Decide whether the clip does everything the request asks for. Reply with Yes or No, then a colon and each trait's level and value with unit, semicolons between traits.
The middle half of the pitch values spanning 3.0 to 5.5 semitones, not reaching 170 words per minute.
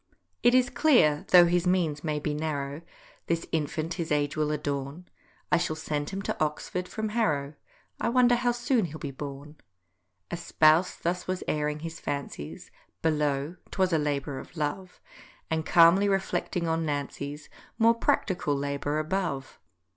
Yes: average, 3.7 semitones; average, 155 wpm